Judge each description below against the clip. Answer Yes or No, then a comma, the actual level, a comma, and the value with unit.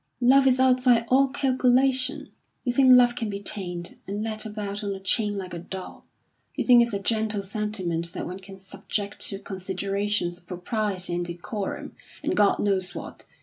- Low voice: No, high, 205 Hz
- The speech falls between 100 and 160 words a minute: No, average, 180 wpm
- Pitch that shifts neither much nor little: Yes, average, 4.1 semitones